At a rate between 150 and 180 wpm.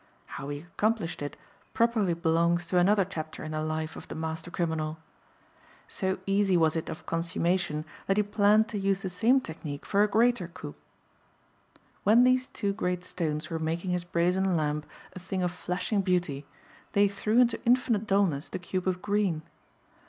Yes: average, 175 wpm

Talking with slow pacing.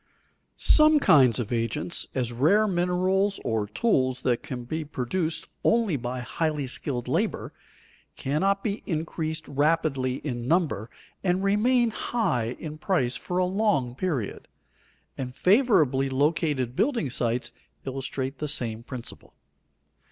Yes: slow, 125 wpm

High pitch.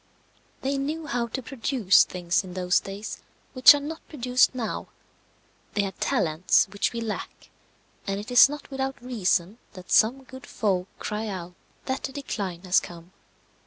Yes: high, 225 Hz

